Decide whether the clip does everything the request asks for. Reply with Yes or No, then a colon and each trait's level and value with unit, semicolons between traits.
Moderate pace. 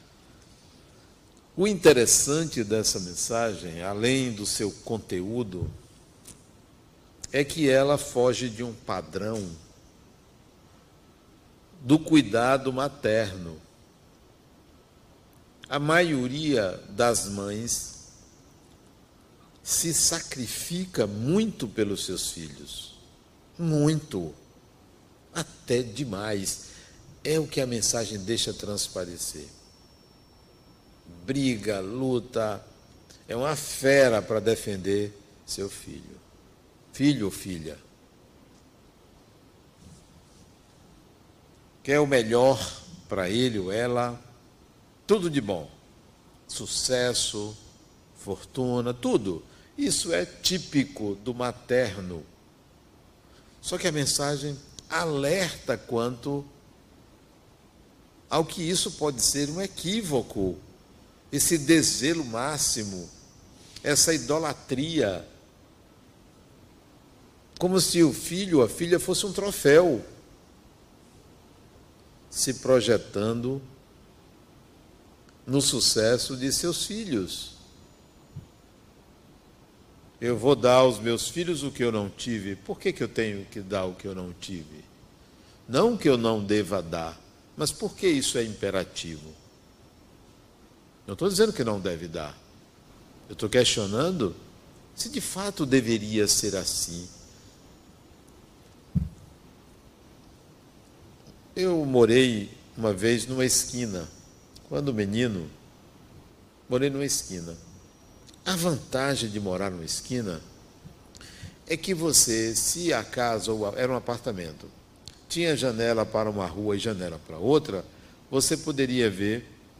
No: slow, 95 wpm